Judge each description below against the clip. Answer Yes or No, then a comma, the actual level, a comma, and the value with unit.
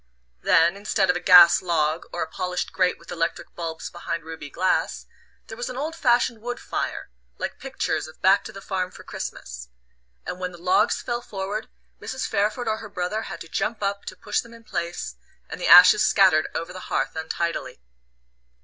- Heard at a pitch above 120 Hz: Yes, medium, 185 Hz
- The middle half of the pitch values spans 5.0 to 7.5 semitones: No, average, 4.0 semitones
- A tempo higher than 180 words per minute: Yes, average, 195 wpm